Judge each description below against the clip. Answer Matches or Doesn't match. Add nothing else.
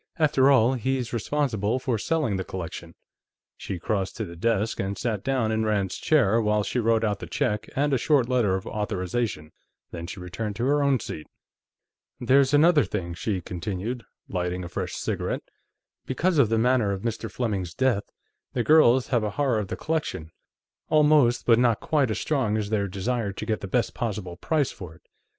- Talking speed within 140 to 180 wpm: Doesn't match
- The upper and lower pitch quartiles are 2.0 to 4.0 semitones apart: Doesn't match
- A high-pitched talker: Doesn't match